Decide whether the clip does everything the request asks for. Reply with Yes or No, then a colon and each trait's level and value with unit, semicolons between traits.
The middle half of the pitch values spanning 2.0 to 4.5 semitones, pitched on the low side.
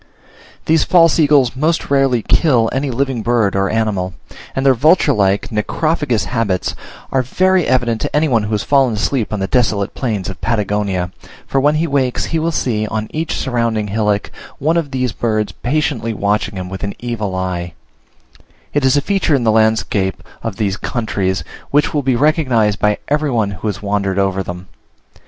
No: average, 5.2 semitones; low, 115 Hz